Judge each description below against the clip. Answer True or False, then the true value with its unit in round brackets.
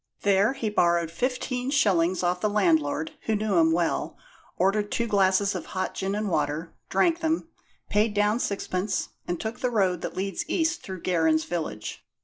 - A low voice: False (195 Hz)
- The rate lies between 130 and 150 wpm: False (170 wpm)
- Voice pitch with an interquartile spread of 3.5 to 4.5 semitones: True (4.1 semitones)